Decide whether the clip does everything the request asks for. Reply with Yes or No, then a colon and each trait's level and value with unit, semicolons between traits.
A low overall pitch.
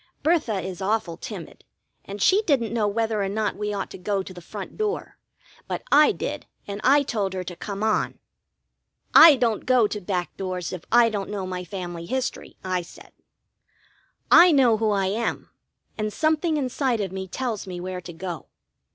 No: high, 205 Hz